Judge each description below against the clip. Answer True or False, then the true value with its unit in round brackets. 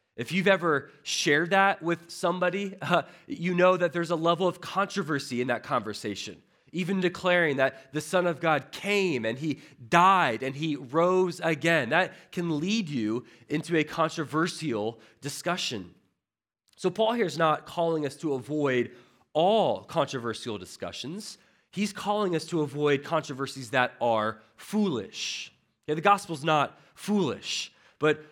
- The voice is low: False (160 Hz)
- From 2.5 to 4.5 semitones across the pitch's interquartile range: False (5.1 semitones)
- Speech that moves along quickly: False (145 wpm)